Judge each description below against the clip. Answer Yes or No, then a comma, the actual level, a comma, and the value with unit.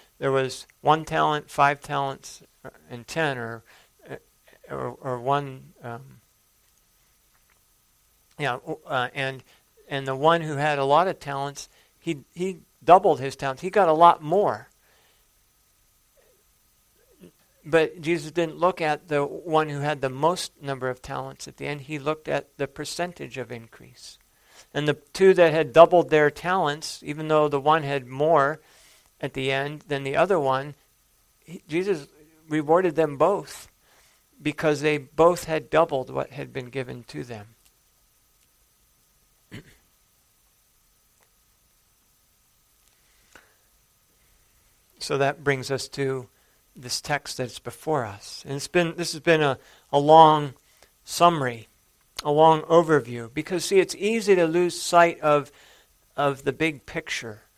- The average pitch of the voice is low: No, medium, 150 Hz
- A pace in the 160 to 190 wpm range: No, slow, 135 wpm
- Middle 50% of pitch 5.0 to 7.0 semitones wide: No, average, 3.3 semitones